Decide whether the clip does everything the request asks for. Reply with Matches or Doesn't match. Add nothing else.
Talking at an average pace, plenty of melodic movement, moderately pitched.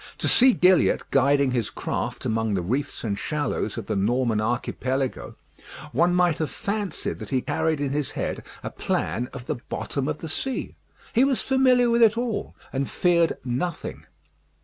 Matches